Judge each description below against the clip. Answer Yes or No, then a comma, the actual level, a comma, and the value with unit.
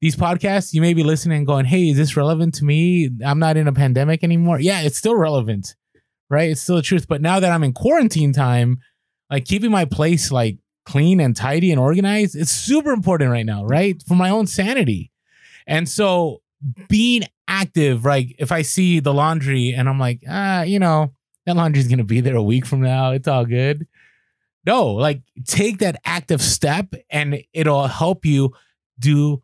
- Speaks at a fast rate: No, average, 195 wpm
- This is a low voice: No, medium, 155 Hz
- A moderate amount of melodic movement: Yes, average, 4.7 semitones